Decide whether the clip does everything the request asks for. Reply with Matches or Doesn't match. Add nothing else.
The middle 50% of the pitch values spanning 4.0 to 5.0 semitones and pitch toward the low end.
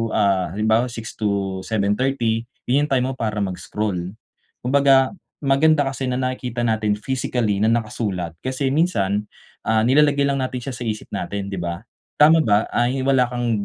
Matches